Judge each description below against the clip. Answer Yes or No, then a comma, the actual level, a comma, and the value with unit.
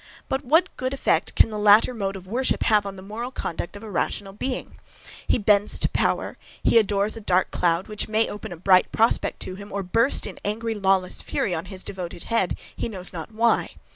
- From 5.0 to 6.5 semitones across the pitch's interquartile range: No, average, 3.2 semitones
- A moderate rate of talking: No, fast, 215 wpm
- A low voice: No, high, 205 Hz